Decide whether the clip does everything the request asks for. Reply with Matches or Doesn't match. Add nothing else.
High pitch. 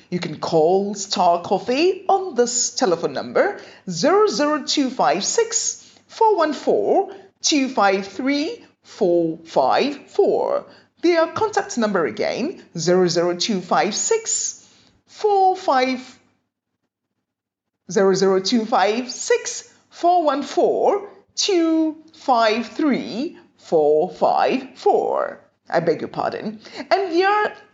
Matches